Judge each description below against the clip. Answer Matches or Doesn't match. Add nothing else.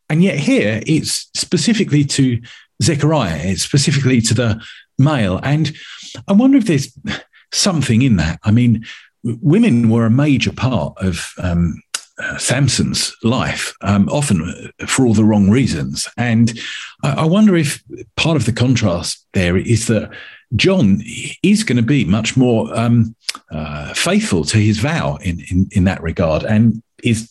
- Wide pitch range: Matches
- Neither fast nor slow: Matches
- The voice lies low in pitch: Matches